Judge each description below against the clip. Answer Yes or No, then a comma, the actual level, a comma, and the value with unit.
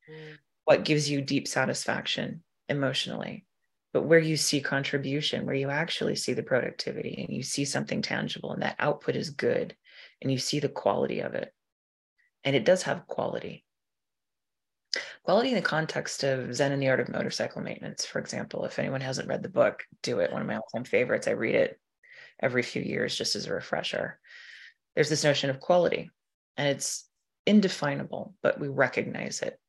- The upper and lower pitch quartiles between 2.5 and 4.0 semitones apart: Yes, average, 3.4 semitones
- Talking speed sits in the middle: Yes, average, 180 wpm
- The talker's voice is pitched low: No, medium, 145 Hz